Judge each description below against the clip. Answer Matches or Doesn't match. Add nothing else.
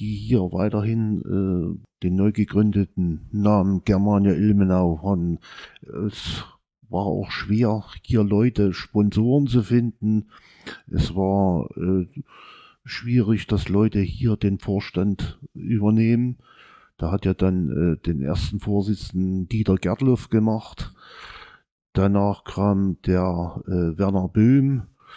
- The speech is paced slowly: Matches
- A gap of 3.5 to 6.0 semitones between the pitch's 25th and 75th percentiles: Doesn't match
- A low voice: Matches